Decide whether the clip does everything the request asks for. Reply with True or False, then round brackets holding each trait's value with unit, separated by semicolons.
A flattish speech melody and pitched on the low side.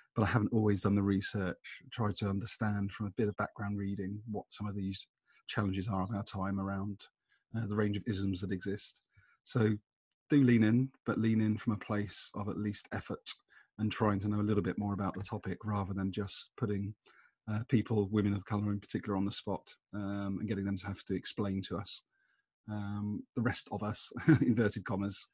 True (1.4 semitones; 105 Hz)